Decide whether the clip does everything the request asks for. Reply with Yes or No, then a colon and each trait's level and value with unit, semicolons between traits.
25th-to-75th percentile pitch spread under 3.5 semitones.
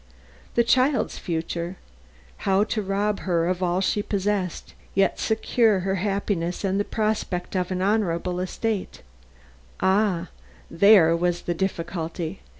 Yes: average, 2.8 semitones